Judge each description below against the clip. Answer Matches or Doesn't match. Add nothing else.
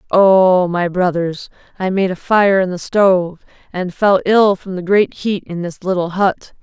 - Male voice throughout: Doesn't match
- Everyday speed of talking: Matches